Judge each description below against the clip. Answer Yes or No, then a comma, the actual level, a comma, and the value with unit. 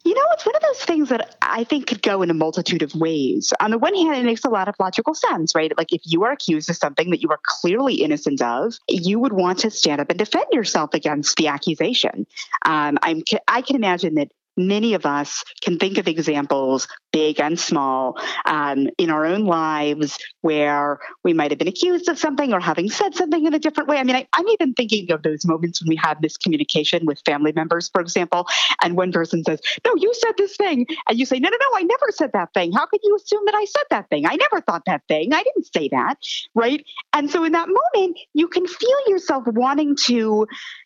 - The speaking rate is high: Yes, fast, 235 wpm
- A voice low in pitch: No, high, 205 Hz